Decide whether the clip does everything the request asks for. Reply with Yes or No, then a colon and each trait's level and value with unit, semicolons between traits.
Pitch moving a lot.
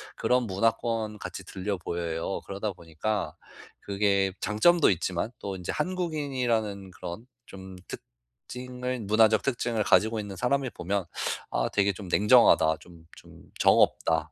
No: average, 4.3 semitones